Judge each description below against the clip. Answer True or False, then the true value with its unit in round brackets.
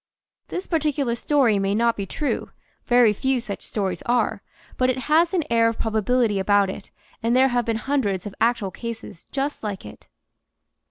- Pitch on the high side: True (230 Hz)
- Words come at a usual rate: True (175 wpm)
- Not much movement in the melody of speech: False (4.1 semitones)